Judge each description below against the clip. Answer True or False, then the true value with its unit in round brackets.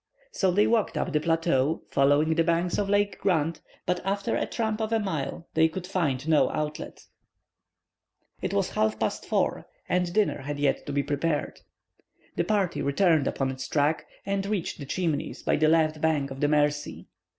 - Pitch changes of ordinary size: True (4.2 semitones)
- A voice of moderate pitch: True (160 Hz)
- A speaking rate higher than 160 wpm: True (185 wpm)